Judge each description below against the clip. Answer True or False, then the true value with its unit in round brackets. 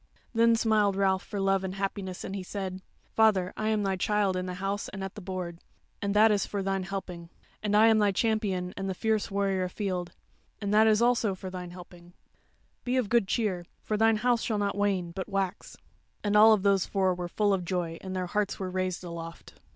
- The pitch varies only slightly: True (2.3 semitones)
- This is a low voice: False (195 Hz)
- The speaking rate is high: True (215 wpm)